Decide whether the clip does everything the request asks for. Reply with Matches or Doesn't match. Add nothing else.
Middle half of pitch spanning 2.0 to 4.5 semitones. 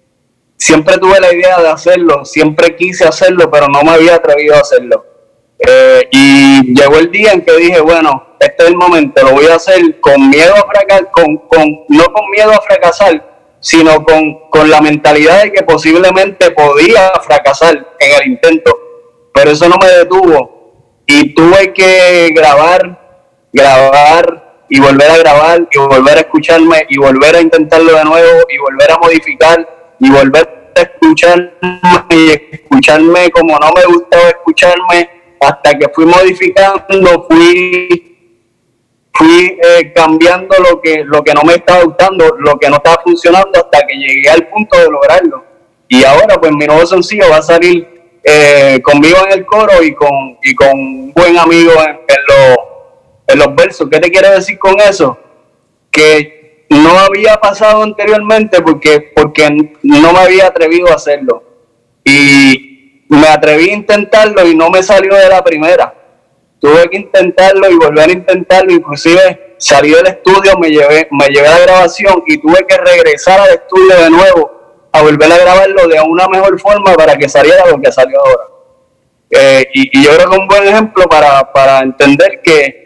Doesn't match